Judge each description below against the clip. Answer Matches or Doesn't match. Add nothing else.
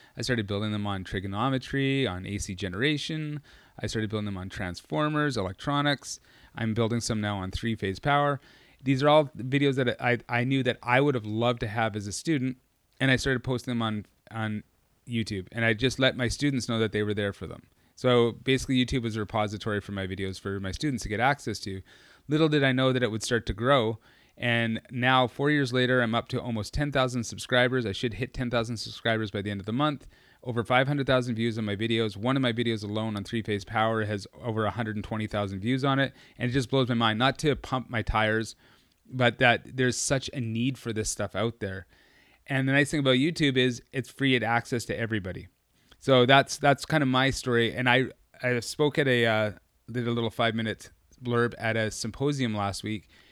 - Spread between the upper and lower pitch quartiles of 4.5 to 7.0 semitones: Doesn't match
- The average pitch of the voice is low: Matches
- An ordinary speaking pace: Doesn't match